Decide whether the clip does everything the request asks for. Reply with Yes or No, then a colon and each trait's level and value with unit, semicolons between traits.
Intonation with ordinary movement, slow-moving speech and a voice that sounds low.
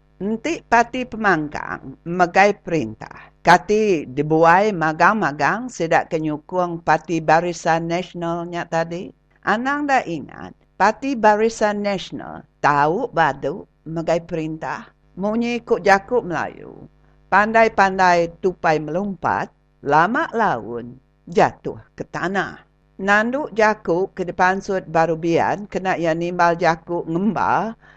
No: average, 4.3 semitones; slow, 95 wpm; medium, 175 Hz